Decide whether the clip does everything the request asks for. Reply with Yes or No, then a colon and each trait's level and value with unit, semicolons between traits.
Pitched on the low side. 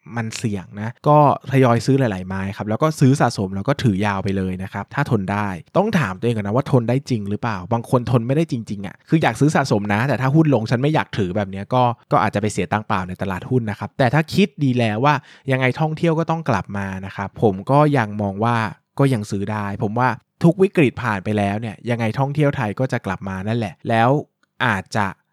Yes: low, 120 Hz